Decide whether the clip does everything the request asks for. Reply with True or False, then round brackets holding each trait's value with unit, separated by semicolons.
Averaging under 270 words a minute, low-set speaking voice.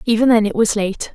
False (260 wpm; 220 Hz)